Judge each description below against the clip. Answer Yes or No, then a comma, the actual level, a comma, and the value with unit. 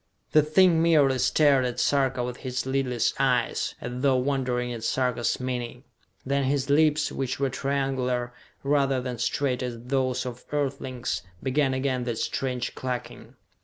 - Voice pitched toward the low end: Yes, low, 130 Hz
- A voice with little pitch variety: Yes, narrow, 1.9 semitones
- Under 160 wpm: Yes, average, 150 wpm